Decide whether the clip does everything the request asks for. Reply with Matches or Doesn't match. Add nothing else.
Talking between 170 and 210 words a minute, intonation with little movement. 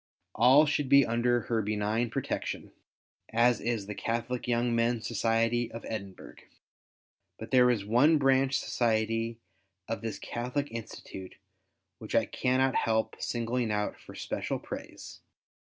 Doesn't match